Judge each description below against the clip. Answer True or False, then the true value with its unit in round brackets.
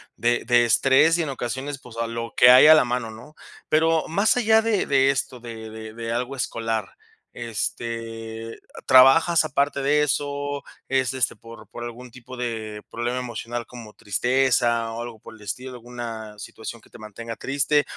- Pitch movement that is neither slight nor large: True (3.0 semitones)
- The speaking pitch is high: False (120 Hz)